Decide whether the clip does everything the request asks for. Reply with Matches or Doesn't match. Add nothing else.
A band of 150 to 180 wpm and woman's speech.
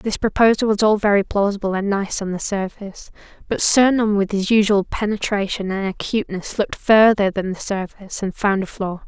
Doesn't match